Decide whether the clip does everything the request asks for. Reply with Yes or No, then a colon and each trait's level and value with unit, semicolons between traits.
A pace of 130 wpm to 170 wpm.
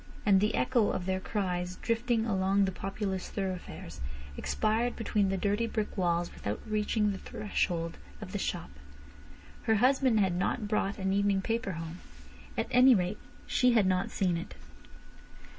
Yes: average, 160 wpm